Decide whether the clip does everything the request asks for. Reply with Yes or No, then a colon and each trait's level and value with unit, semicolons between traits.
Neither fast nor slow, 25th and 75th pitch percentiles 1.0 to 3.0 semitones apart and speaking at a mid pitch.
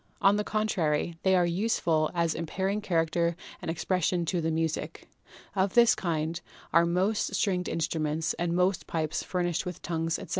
Yes: average, 160 wpm; narrow, 2.5 semitones; medium, 170 Hz